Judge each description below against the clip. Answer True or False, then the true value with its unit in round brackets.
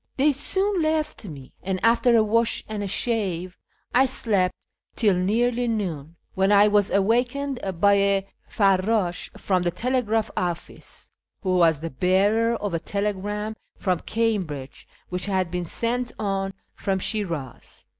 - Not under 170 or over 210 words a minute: False (140 wpm)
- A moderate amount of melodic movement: True (3.9 semitones)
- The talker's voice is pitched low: False (200 Hz)